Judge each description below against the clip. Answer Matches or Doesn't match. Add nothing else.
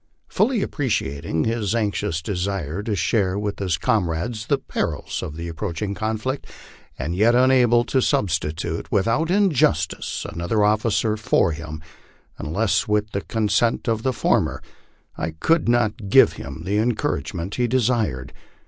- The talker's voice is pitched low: Matches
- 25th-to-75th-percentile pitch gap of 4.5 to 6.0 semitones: Matches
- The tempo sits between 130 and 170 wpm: Matches